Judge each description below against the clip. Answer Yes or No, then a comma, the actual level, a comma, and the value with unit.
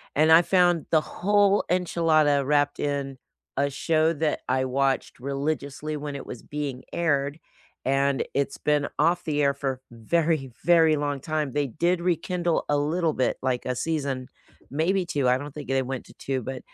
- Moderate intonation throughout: Yes, average, 3.0 semitones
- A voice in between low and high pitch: Yes, medium, 145 Hz